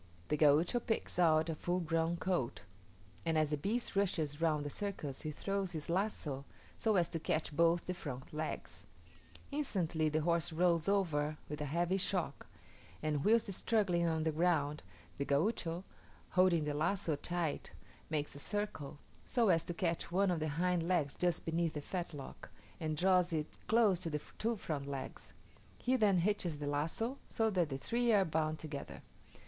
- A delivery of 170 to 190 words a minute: Yes, average, 175 wpm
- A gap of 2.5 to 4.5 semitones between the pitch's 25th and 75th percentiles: Yes, average, 3.5 semitones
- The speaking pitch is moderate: Yes, medium, 165 Hz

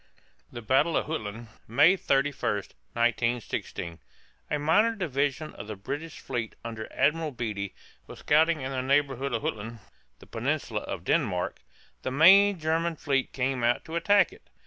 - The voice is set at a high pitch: No, low, 135 Hz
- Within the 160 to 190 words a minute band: No, average, 150 wpm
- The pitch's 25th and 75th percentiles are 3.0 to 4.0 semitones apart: No, wide, 5.4 semitones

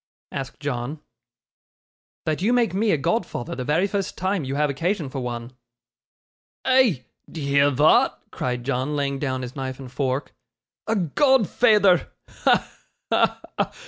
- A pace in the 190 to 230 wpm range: No, average, 145 wpm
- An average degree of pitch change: No, wide, 6.7 semitones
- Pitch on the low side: No, medium, 145 Hz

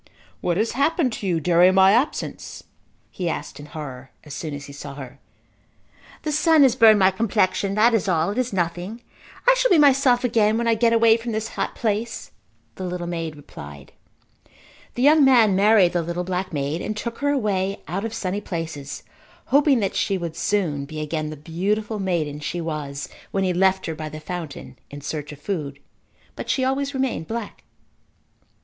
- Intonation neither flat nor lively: No, wide, 6.3 semitones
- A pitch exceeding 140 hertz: Yes, high, 190 Hz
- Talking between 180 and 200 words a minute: Yes, average, 190 wpm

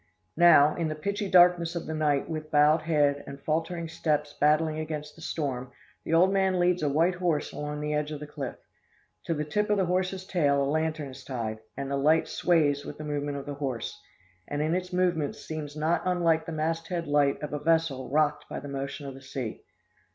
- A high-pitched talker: No, medium, 155 Hz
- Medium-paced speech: No, fast, 215 wpm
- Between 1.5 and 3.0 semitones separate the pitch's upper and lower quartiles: Yes, narrow, 2.5 semitones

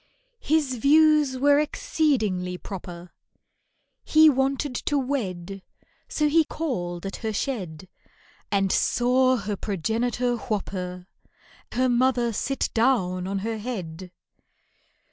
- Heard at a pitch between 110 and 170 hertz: No, high, 235 Hz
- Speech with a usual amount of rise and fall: No, wide, 6.2 semitones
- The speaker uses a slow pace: Yes, slow, 110 wpm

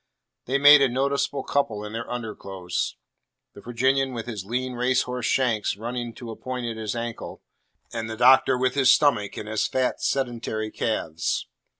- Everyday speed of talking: Yes, average, 170 wpm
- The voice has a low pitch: Yes, low, 120 Hz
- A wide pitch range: No, average, 2.8 semitones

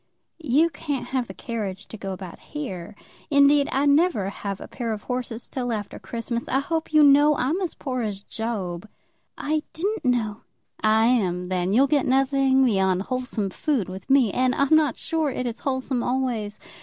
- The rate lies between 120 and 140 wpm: No, average, 185 wpm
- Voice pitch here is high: Yes, very high, 250 Hz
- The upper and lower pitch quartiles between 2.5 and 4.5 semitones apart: No, average, 5.2 semitones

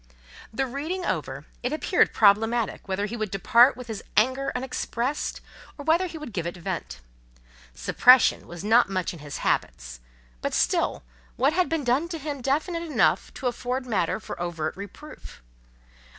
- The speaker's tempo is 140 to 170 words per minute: Yes, average, 165 wpm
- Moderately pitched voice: No, high, 245 Hz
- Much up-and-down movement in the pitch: Yes, wide, 6.6 semitones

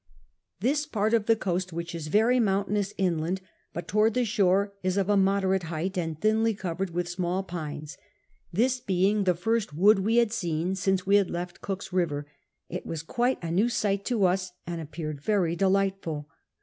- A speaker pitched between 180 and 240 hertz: Yes, high, 190 Hz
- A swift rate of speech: No, average, 185 wpm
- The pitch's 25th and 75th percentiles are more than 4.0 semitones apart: No, average, 3.3 semitones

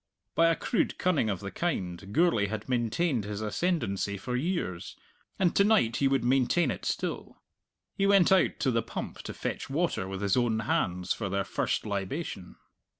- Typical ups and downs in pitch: No, wide, 9.0 semitones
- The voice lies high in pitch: No, low, 120 Hz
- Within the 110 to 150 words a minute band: No, average, 180 wpm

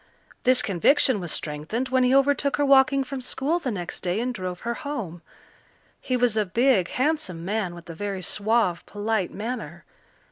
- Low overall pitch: No, high, 230 Hz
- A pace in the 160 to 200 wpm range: Yes, average, 175 wpm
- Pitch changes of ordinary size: No, wide, 6.2 semitones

